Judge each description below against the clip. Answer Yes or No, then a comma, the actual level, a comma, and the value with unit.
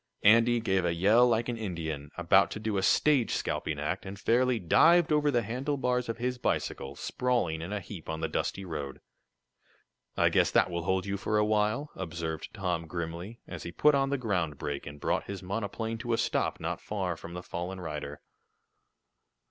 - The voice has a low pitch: Yes, low, 100 Hz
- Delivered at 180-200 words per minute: Yes, average, 195 wpm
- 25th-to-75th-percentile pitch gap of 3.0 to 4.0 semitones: No, wide, 5.6 semitones